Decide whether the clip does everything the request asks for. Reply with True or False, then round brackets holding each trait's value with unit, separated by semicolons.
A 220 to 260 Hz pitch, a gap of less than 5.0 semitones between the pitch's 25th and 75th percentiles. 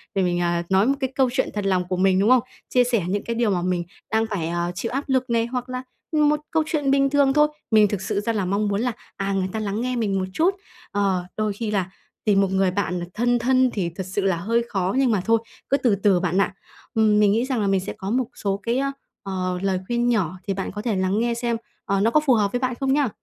False (210 Hz; 4.4 semitones)